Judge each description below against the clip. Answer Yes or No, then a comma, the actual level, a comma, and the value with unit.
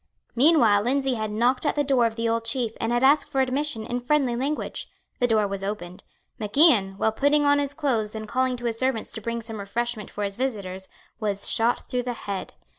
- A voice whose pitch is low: No, high, 235 Hz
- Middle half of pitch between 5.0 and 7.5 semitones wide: No, average, 3.8 semitones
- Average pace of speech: No, fast, 220 wpm